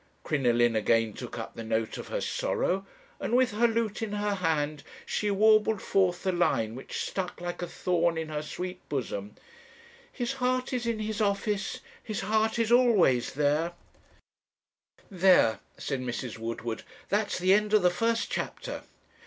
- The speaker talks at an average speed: Yes, average, 160 wpm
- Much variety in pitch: Yes, wide, 6.9 semitones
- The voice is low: No, medium, 185 Hz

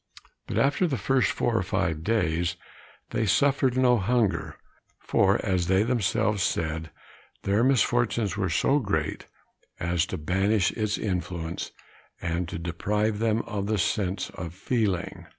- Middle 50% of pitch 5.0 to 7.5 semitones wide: No, average, 4.6 semitones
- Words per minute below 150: Yes, average, 140 wpm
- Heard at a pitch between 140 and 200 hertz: No, low, 100 Hz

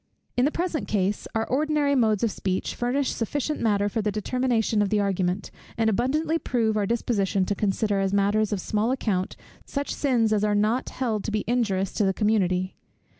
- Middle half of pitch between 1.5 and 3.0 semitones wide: No, average, 3.6 semitones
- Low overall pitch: No, high, 215 Hz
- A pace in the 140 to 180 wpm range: No, average, 190 wpm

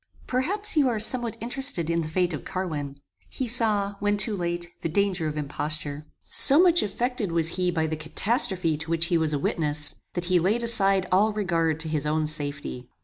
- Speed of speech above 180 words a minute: Yes, average, 200 wpm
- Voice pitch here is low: No, medium, 175 Hz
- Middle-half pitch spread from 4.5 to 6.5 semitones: Yes, average, 5.3 semitones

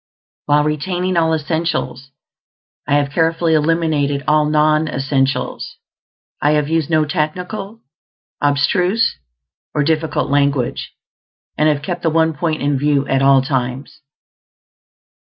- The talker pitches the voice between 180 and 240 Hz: No, medium, 150 Hz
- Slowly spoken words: Yes, slow, 120 wpm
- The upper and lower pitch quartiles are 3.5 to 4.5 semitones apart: No, narrow, 2.4 semitones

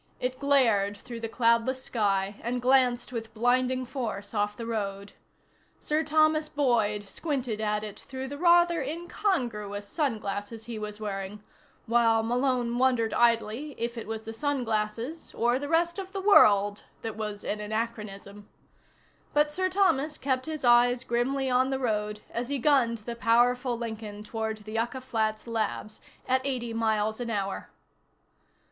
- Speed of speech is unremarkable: Yes, average, 155 wpm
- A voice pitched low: No, high, 235 Hz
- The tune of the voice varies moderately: Yes, average, 3.6 semitones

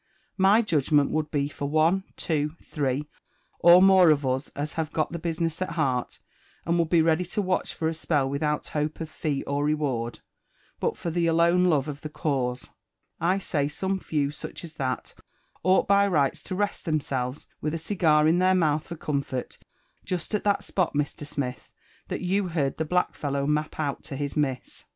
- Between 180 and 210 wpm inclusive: Yes, average, 195 wpm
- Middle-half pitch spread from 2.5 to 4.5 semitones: Yes, average, 3.3 semitones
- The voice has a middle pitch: Yes, medium, 155 Hz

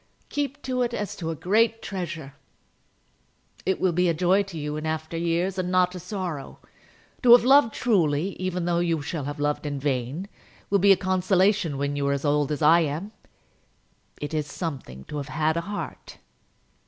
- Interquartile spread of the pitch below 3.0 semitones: No, average, 4.5 semitones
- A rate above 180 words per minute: Yes, average, 190 wpm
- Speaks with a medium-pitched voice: Yes, medium, 170 Hz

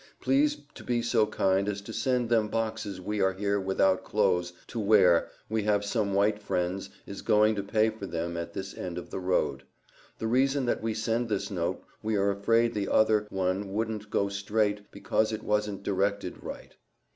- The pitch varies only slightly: Yes, narrow, 2.2 semitones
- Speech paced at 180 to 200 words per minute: Yes, average, 190 wpm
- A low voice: Yes, low, 105 Hz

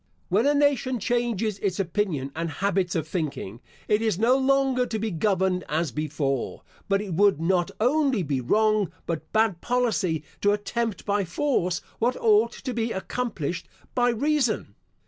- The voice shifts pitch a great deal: Yes, wide, 5.7 semitones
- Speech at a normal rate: Yes, average, 160 wpm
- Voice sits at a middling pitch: No, high, 205 Hz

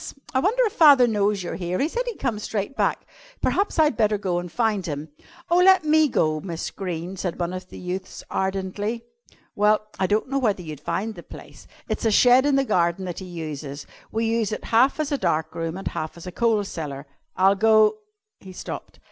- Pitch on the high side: Yes, high, 205 Hz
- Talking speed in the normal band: No, fast, 215 wpm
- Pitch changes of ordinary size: No, wide, 5.8 semitones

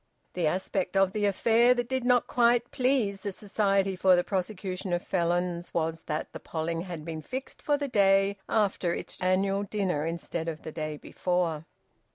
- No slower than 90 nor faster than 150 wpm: No, average, 180 wpm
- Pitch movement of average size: Yes, average, 3.6 semitones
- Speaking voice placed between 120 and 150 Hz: No, high, 190 Hz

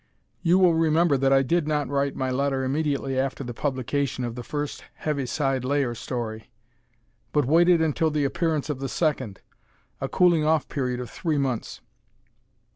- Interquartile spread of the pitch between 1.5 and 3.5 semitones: Yes, average, 3.1 semitones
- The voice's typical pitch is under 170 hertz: Yes, medium, 140 Hz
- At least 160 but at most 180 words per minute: Yes, average, 165 wpm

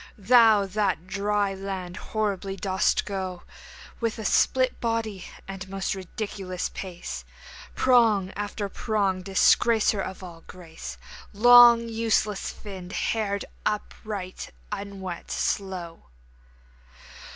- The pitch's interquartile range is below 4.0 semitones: Yes, narrow, 2.5 semitones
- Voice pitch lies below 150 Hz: No, high, 200 Hz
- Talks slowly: Yes, slow, 105 wpm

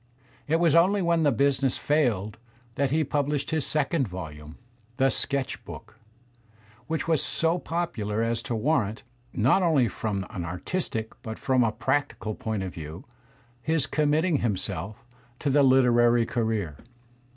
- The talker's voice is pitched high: No, low, 130 Hz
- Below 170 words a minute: Yes, average, 150 wpm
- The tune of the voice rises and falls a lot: Yes, wide, 5.8 semitones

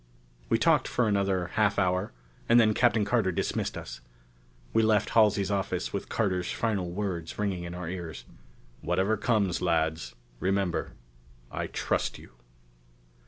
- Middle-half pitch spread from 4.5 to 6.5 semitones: No, average, 3.1 semitones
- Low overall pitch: Yes, very low, 95 Hz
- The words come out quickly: No, average, 140 wpm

